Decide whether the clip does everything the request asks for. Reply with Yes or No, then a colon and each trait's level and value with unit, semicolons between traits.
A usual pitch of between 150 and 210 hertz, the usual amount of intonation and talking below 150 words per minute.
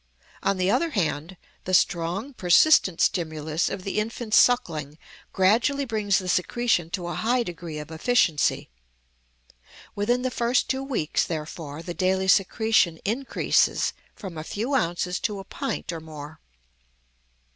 No: medium, 185 Hz; wide, 5.9 semitones; average, 140 wpm